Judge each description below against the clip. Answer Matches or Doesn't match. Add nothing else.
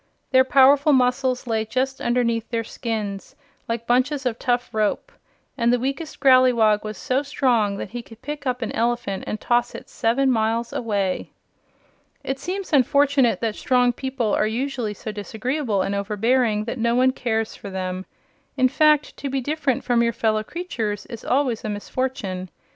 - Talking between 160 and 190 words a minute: Matches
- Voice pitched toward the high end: Matches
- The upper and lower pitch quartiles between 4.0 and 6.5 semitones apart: Doesn't match